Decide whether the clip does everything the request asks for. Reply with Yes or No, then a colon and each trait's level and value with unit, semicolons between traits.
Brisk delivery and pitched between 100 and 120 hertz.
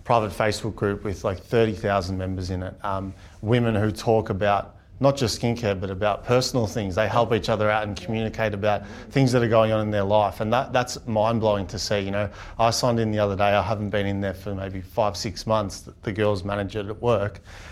Yes: fast, 225 wpm; low, 105 Hz